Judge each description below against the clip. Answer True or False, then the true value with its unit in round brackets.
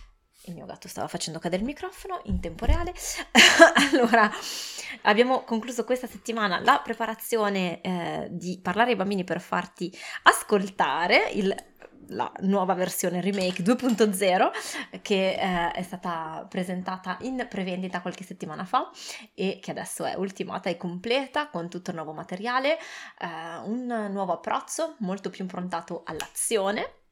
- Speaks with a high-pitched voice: True (195 Hz)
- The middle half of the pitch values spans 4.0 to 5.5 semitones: True (4.6 semitones)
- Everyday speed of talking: True (140 wpm)